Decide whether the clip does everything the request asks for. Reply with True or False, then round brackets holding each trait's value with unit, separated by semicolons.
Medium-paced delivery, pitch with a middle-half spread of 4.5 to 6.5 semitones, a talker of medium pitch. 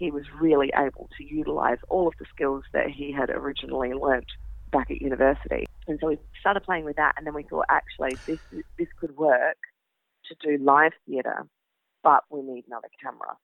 False (190 wpm; 3.8 semitones; 145 Hz)